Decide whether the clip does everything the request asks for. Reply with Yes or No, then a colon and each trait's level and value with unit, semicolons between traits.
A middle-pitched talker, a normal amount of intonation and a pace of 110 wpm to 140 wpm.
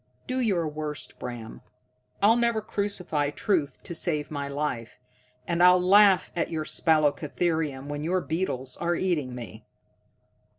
Yes: medium, 160 Hz; average, 4.2 semitones; slow, 135 wpm